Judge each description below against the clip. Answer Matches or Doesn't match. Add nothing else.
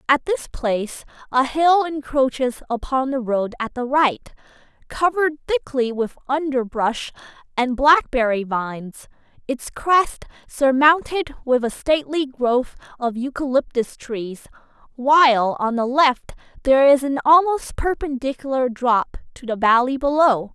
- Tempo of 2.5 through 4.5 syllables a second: Matches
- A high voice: Matches